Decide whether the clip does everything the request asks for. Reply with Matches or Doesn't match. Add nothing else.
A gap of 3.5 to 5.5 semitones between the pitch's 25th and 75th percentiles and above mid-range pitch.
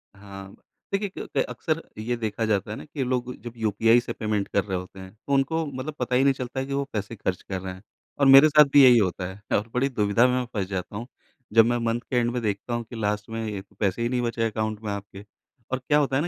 Doesn't match